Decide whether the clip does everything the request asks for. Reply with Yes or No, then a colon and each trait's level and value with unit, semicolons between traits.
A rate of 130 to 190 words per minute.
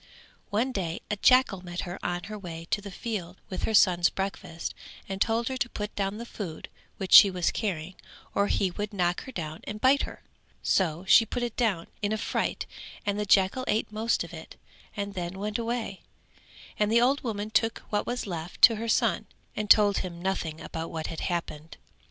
No: fast, 205 wpm